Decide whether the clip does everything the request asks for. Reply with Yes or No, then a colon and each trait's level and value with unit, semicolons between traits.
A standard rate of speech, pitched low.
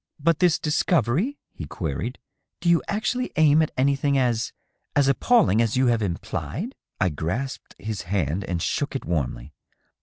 Yes: average, 190 wpm; low, 130 Hz